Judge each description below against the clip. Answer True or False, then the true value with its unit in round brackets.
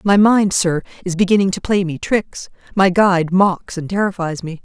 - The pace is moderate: True (195 wpm)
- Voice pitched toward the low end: False (185 Hz)